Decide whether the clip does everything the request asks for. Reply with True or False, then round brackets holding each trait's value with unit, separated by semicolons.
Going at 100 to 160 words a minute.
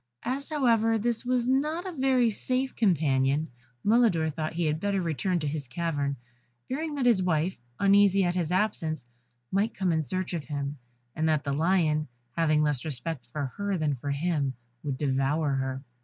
False (175 wpm)